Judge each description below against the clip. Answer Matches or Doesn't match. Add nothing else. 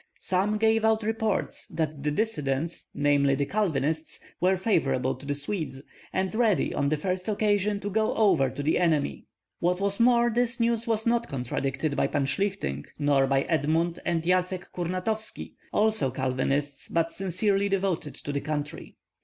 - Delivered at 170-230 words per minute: Doesn't match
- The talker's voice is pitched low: Doesn't match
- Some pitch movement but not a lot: Doesn't match